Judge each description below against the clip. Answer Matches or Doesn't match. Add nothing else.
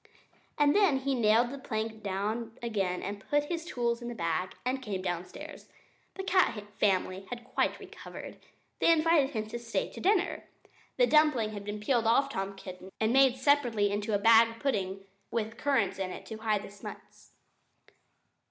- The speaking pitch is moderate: Doesn't match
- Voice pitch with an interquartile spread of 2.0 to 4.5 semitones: Doesn't match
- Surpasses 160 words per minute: Matches